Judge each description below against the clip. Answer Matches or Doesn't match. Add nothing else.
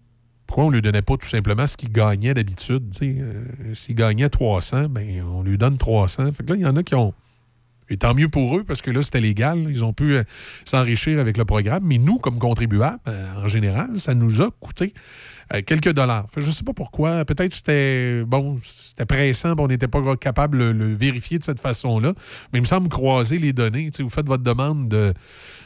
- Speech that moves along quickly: Matches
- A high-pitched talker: Doesn't match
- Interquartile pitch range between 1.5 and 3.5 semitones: Doesn't match